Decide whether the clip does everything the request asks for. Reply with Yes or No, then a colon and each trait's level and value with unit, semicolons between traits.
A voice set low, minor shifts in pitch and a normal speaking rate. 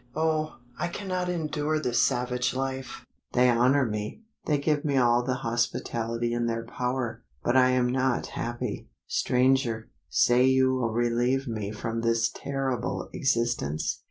Yes: low, 125 Hz; narrow, 2.2 semitones; average, 145 wpm